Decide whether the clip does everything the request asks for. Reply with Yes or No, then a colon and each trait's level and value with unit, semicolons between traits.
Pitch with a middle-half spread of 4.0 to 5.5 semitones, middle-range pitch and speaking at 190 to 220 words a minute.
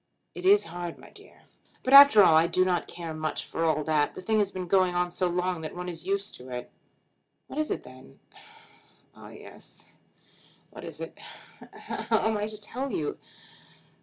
Yes: average, 4.3 semitones; medium, 180 Hz; average, 195 wpm